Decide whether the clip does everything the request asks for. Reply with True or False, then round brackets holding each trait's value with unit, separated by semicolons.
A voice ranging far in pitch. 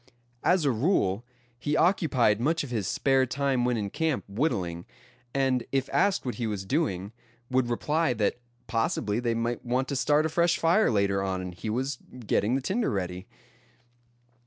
True (5.8 semitones)